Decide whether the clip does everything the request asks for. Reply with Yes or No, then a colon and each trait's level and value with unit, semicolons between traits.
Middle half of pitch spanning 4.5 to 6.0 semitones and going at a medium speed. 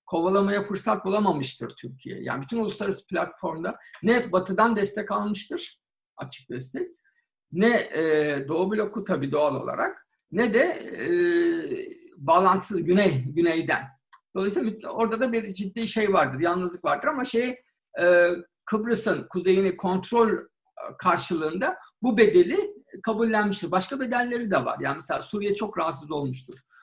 Yes: average, 4.9 semitones; average, 120 wpm